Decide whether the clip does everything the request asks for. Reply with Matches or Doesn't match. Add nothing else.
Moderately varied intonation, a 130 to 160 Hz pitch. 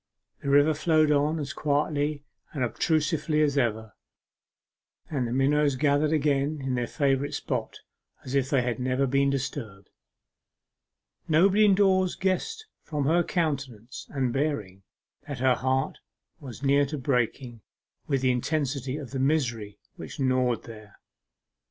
Matches